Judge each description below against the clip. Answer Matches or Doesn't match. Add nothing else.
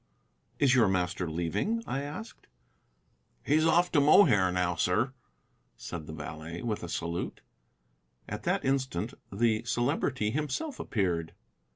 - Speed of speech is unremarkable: Doesn't match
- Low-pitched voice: Matches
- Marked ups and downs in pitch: Matches